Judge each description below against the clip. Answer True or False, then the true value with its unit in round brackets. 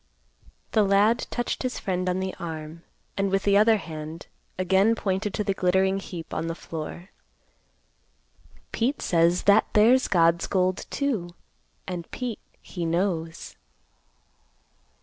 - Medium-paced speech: False (130 wpm)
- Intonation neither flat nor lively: True (3.4 semitones)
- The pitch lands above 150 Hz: True (190 Hz)